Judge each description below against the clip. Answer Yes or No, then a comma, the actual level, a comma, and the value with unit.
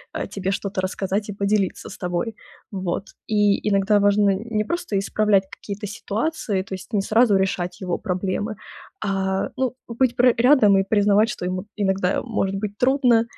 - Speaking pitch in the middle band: No, high, 205 Hz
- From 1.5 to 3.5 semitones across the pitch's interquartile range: Yes, narrow, 2.4 semitones